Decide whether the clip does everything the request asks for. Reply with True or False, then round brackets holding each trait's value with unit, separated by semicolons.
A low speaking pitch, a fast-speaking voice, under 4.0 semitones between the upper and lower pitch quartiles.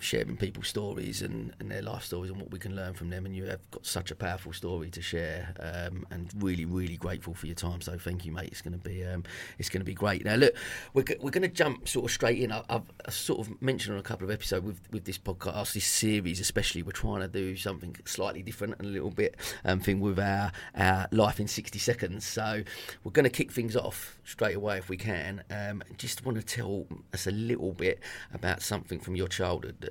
True (95 Hz; 245 wpm; 2.6 semitones)